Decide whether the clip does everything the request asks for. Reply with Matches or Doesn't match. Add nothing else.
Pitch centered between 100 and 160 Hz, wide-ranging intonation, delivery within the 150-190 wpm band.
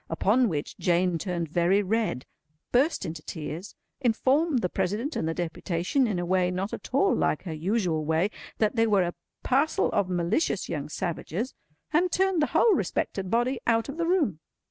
Doesn't match